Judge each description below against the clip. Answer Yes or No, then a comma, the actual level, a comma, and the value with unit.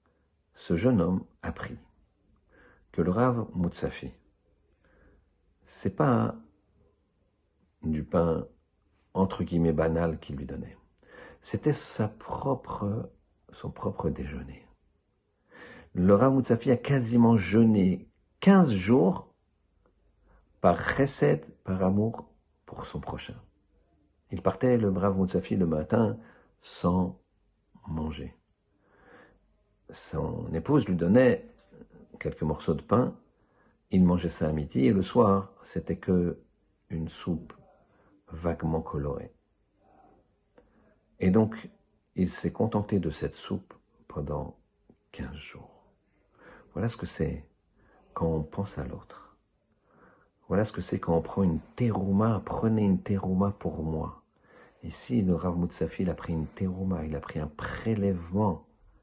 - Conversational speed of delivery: No, slow, 120 wpm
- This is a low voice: Yes, very low, 95 Hz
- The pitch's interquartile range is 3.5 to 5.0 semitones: Yes, average, 4.3 semitones